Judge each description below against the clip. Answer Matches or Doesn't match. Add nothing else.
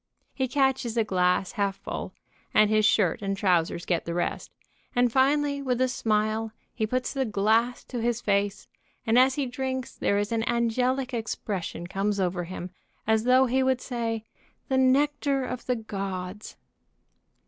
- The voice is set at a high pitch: Matches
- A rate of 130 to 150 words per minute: Doesn't match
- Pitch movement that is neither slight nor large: Matches